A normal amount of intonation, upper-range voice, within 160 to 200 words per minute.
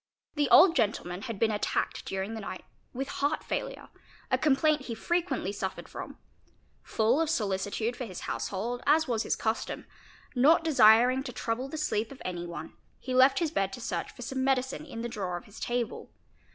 Yes: average, 4.7 semitones; high, 240 Hz; average, 190 wpm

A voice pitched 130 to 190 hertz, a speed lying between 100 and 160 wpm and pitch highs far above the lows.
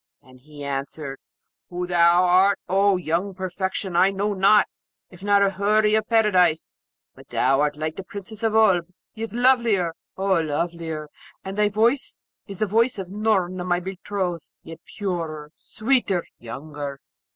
No: medium, 185 Hz; average, 150 wpm; average, 3.9 semitones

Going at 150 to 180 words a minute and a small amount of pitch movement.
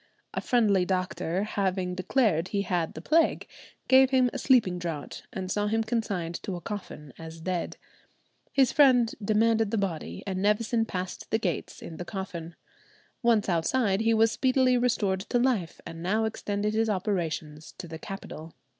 No: average, 165 wpm; average, 4.2 semitones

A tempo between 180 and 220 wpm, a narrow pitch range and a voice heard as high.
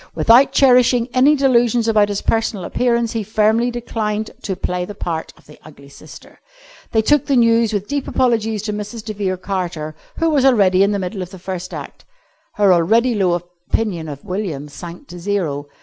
No: average, 190 wpm; average, 4.6 semitones; high, 210 Hz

